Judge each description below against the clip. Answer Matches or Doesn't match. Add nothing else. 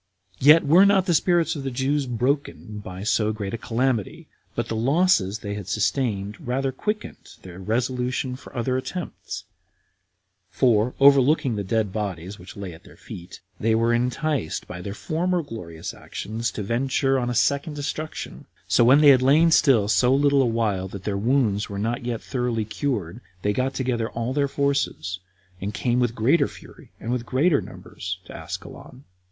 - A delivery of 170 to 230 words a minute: Matches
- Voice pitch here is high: Doesn't match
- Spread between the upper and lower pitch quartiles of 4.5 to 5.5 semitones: Matches